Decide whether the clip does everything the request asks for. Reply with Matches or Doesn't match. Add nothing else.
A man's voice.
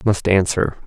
Matches